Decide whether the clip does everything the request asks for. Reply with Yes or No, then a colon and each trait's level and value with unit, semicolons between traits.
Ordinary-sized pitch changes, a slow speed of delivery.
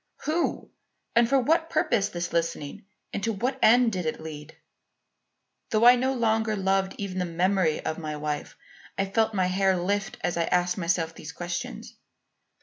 No: average, 4.9 semitones; average, 170 wpm